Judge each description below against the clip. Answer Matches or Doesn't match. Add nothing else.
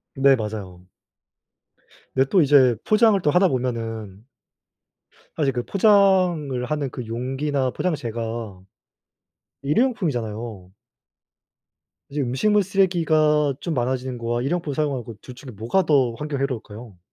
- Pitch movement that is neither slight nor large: Matches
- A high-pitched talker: Doesn't match